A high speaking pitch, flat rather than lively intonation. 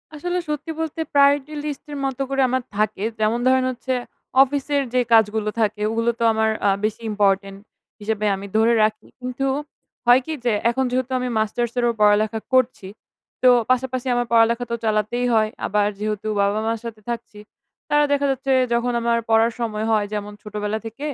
No: high, 230 Hz; average, 3.3 semitones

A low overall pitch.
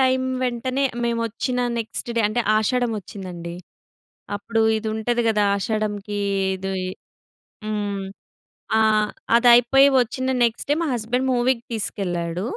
No: high, 230 Hz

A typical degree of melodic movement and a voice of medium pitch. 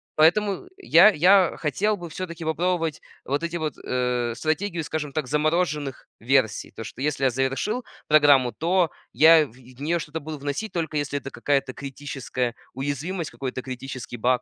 Yes: average, 4.1 semitones; medium, 150 Hz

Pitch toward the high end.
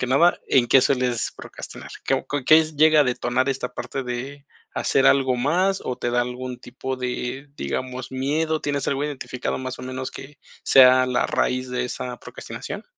No: low, 130 Hz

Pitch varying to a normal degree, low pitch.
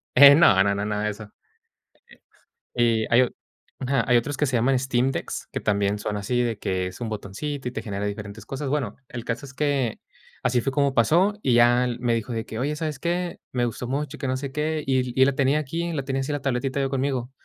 Yes: average, 3.5 semitones; low, 130 Hz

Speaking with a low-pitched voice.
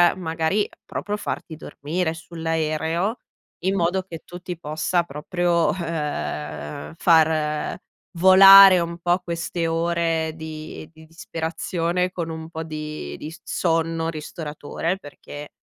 No: medium, 165 Hz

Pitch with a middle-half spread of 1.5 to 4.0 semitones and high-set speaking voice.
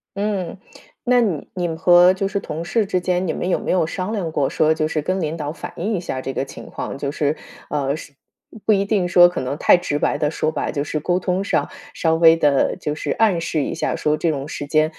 No: average, 3.5 semitones; medium, 165 Hz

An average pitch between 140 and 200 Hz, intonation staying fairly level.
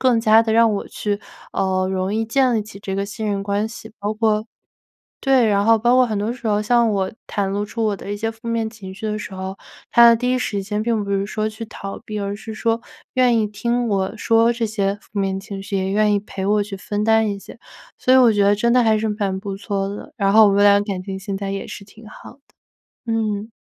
No: high, 210 Hz; narrow, 2.2 semitones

